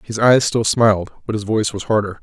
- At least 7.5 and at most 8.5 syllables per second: No, 6.1 syllables/s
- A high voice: No, low, 110 Hz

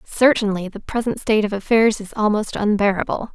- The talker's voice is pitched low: No, high, 210 Hz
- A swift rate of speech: No, average, 160 wpm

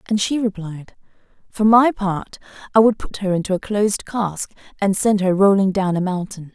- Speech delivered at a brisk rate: No, average, 195 wpm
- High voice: Yes, high, 200 Hz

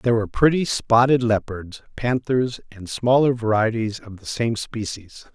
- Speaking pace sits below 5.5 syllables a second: Yes, 4.7 syllables/s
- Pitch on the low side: Yes, low, 115 Hz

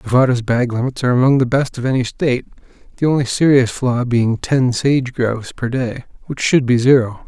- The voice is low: Yes, low, 125 Hz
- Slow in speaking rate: No, average, 200 wpm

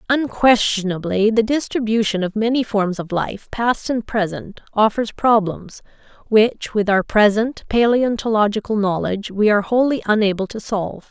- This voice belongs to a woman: Yes, female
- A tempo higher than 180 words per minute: No, slow, 135 wpm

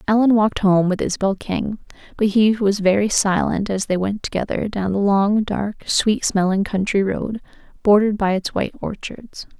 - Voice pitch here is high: Yes, high, 205 Hz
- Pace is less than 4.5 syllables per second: No, 5.0 syllables/s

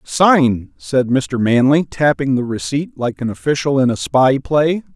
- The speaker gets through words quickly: No, average, 170 wpm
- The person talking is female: No, male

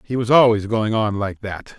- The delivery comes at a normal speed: No, fast, 235 wpm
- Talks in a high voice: No, low, 110 Hz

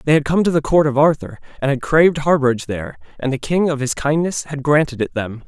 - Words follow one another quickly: Yes, fast, 250 wpm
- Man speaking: Yes, male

